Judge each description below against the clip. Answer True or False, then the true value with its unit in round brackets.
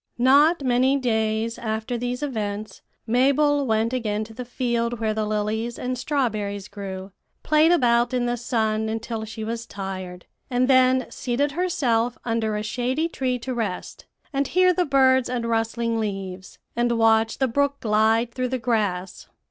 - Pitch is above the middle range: True (235 Hz)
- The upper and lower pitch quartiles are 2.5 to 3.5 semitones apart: True (2.9 semitones)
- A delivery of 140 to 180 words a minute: True (160 wpm)